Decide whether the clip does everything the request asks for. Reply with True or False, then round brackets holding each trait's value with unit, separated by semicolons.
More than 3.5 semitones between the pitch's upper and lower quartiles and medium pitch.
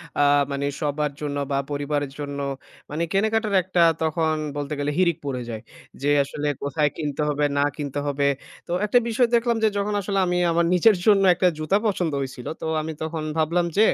True (4.5 semitones; 155 Hz)